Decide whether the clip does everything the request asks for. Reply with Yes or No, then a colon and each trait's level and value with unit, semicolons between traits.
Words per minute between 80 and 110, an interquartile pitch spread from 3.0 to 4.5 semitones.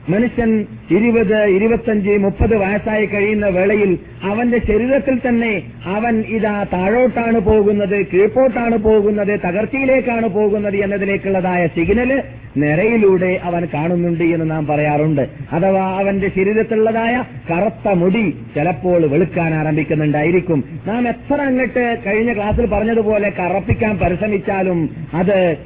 Yes: average, 100 wpm; average, 4.0 semitones